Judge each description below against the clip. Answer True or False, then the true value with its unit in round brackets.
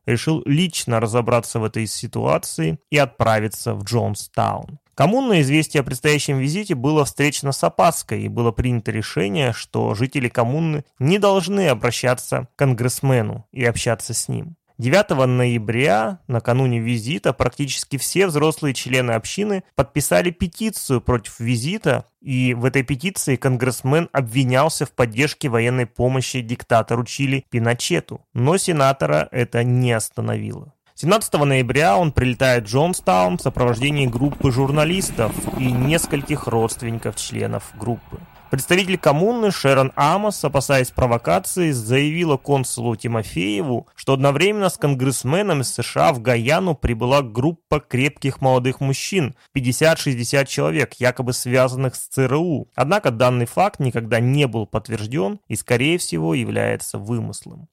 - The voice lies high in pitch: False (130 Hz)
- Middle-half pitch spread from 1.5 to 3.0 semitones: False (3.9 semitones)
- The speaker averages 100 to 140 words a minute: True (125 wpm)